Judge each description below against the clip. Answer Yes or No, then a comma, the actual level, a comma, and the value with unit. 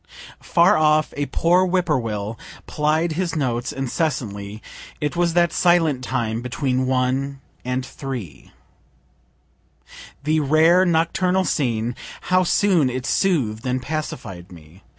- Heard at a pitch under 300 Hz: Yes, medium, 140 Hz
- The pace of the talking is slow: Yes, slow, 125 wpm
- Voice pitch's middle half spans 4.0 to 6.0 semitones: Yes, wide, 5.5 semitones